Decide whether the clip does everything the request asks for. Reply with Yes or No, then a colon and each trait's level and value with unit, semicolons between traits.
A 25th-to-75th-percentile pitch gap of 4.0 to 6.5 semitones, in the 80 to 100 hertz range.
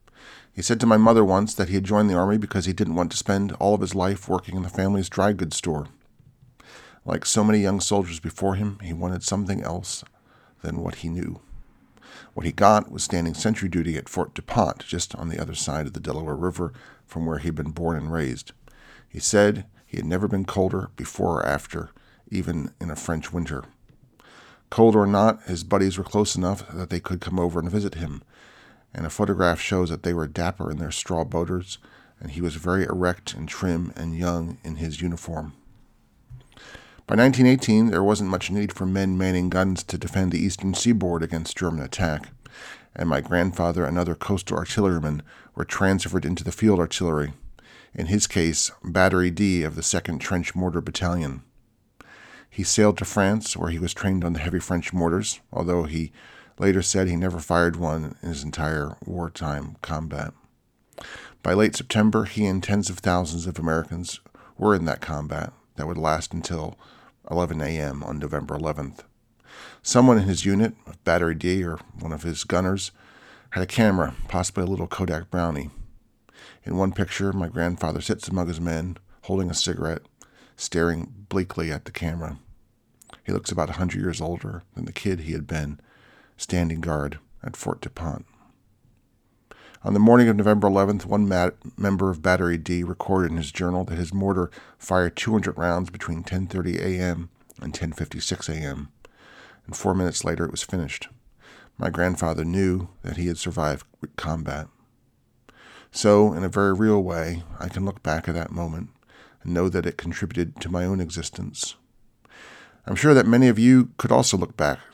No: average, 2.9 semitones; very low, 90 Hz